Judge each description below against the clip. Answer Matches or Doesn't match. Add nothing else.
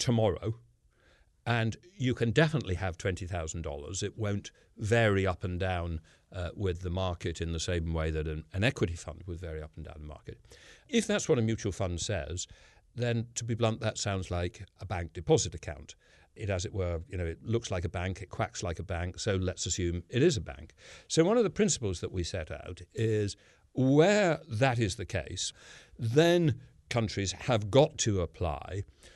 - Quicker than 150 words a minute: Matches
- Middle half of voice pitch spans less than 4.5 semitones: Doesn't match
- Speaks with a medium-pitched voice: Doesn't match